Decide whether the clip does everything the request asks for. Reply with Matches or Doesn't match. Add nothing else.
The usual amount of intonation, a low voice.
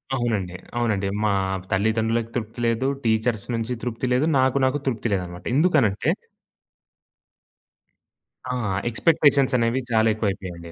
Matches